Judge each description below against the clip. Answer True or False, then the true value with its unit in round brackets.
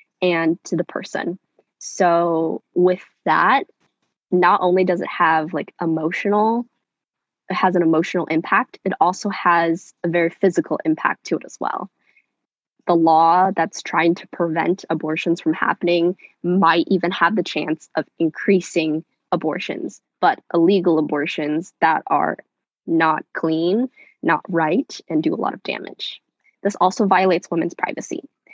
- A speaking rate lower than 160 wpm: True (140 wpm)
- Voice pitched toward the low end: False (170 Hz)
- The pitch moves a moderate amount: False (2.2 semitones)